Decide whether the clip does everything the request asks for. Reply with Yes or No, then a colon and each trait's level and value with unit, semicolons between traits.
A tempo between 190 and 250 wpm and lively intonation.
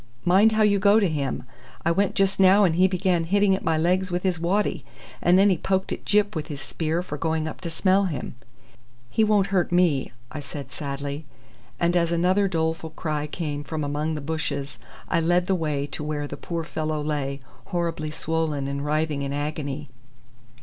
No: average, 200 wpm; average, 3.8 semitones